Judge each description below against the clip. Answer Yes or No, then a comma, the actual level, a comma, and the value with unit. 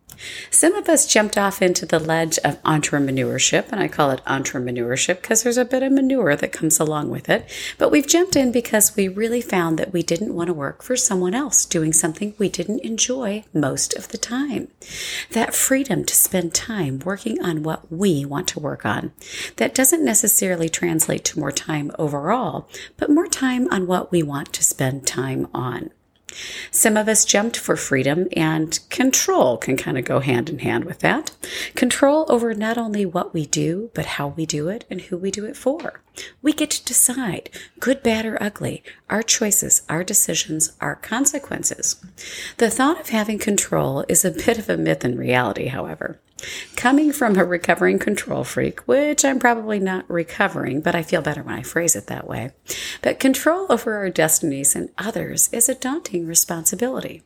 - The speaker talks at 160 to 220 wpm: Yes, average, 190 wpm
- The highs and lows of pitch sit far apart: Yes, wide, 7.4 semitones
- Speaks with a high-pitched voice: Yes, high, 195 Hz